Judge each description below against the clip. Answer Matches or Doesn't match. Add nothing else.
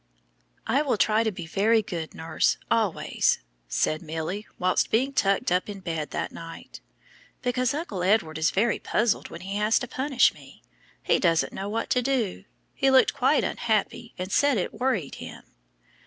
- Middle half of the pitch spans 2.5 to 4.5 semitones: Doesn't match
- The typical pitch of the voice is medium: Doesn't match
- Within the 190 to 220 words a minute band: Doesn't match